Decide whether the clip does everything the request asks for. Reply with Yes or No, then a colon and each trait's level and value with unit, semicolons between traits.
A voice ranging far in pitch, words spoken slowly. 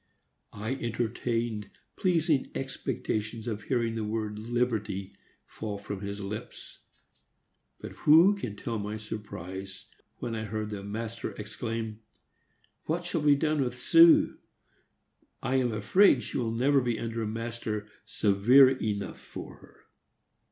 No: average, 3.5 semitones; slow, 130 wpm